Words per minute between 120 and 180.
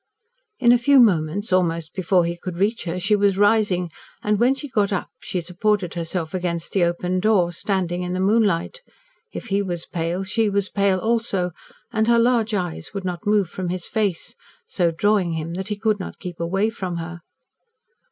No: average, 190 wpm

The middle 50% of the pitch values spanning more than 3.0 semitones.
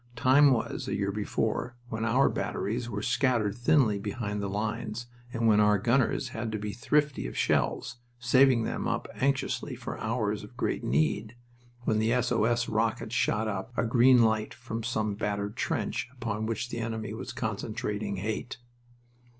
No: narrow, 2.6 semitones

